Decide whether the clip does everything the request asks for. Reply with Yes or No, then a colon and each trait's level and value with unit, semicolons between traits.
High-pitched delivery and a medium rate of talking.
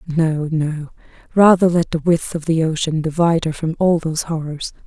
No: medium, 160 Hz; average, 185 wpm